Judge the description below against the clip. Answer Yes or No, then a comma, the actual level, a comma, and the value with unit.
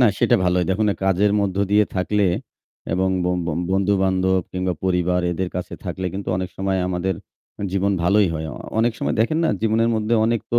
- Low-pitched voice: Yes, very low, 95 Hz